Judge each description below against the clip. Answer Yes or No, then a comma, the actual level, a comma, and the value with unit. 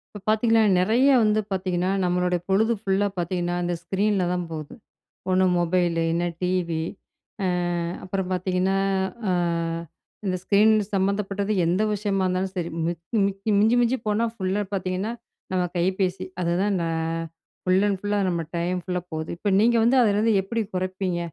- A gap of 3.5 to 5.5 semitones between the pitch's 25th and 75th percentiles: No, narrow, 2.4 semitones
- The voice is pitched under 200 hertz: Yes, high, 190 Hz